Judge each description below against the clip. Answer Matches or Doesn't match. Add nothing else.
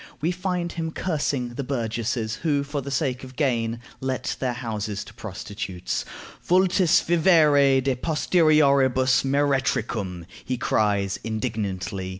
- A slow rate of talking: Matches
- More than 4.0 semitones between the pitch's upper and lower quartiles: Matches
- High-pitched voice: Doesn't match